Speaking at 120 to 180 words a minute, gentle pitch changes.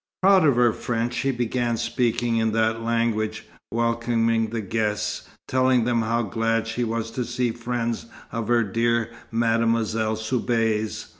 Yes: average, 145 wpm; narrow, 1.1 semitones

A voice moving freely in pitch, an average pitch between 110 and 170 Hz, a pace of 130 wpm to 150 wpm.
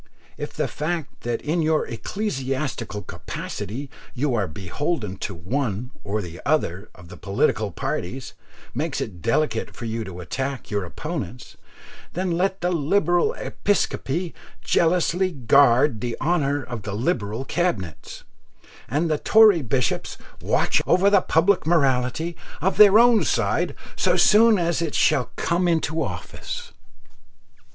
Yes: wide, 7.3 semitones; medium, 140 Hz; slow, 135 wpm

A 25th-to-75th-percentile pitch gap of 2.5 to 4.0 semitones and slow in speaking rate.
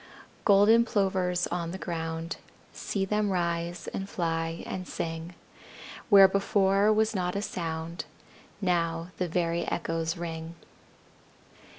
Yes: average, 2.8 semitones; slow, 115 wpm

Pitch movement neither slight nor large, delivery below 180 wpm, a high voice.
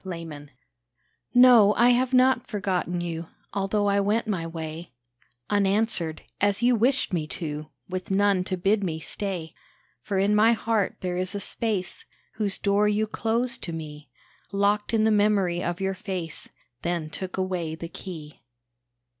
Yes: average, 3.6 semitones; average, 160 wpm; high, 195 Hz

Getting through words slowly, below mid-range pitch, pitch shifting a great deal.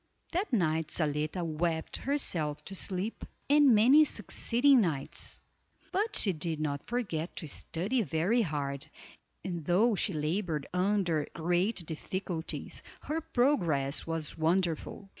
No: slow, 120 wpm; medium, 175 Hz; wide, 6.1 semitones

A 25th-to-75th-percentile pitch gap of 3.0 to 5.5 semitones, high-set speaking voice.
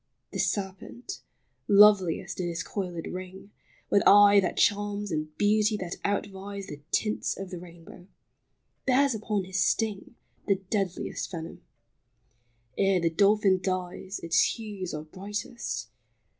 No: narrow, 2.4 semitones; high, 195 Hz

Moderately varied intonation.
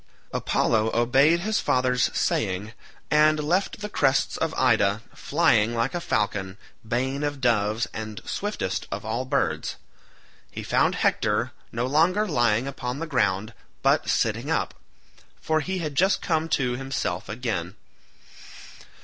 No: wide, 5.9 semitones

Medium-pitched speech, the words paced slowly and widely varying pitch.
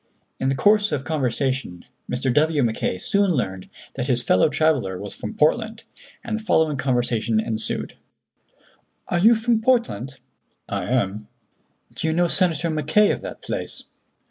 No: medium, 145 Hz; average, 150 wpm; wide, 6.8 semitones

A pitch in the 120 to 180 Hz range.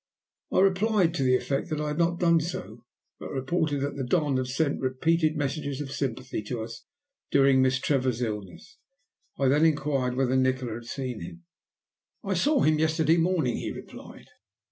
Yes: medium, 140 Hz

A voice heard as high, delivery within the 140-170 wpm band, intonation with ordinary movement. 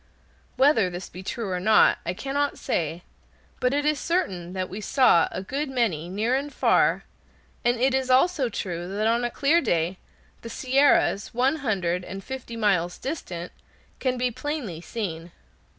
No: high, 230 Hz; average, 165 wpm; wide, 6.6 semitones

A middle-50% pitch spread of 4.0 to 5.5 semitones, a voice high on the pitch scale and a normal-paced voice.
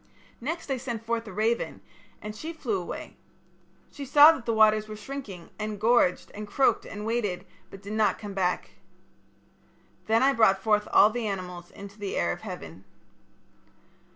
No: average, 3.1 semitones; high, 215 Hz; average, 170 wpm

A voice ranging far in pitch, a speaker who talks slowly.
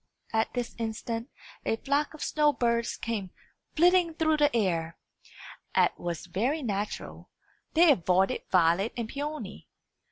Yes: wide, 7.3 semitones; slow, 130 wpm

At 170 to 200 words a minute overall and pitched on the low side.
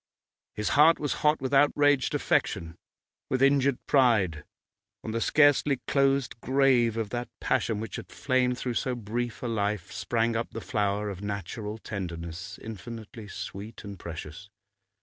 No: average, 150 wpm; low, 115 Hz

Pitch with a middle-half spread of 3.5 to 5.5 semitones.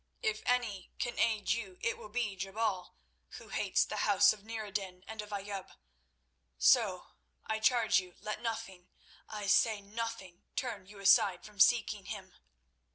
No: average, 2.7 semitones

